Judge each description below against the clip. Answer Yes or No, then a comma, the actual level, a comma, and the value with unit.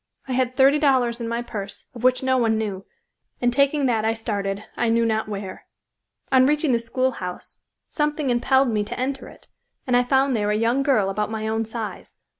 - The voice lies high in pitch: Yes, high, 235 Hz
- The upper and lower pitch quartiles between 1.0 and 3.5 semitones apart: Yes, average, 3.2 semitones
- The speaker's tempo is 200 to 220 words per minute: Yes, fast, 205 wpm